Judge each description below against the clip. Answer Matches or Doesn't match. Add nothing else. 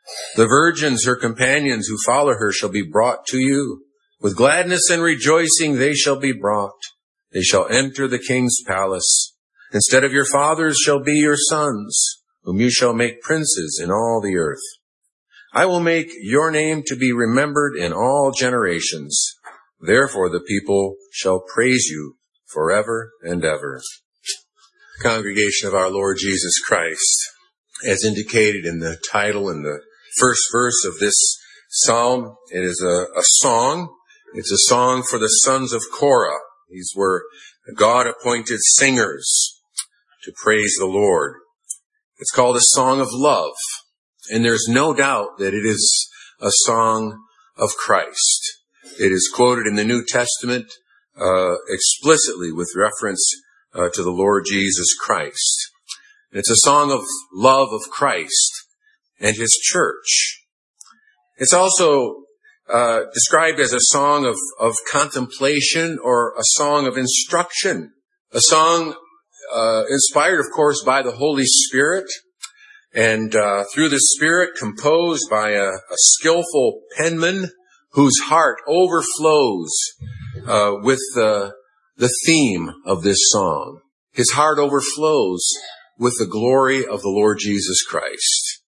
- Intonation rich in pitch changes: Matches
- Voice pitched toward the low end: Matches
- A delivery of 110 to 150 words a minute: Matches